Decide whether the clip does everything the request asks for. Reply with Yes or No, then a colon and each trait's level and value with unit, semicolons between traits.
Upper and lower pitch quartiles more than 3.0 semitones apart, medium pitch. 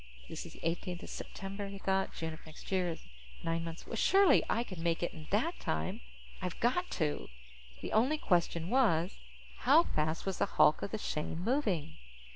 Yes: average, 5.1 semitones; medium, 180 Hz